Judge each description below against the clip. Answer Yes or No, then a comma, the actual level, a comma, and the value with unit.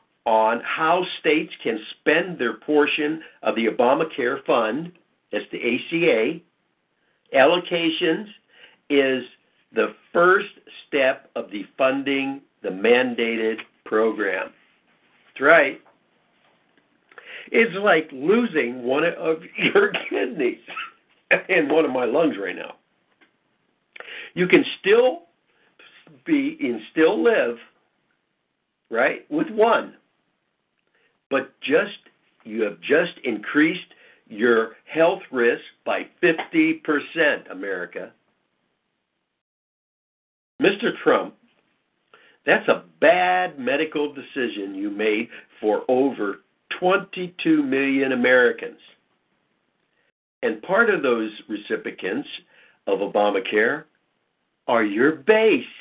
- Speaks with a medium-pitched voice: Yes, medium, 160 Hz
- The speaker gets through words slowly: Yes, slow, 95 wpm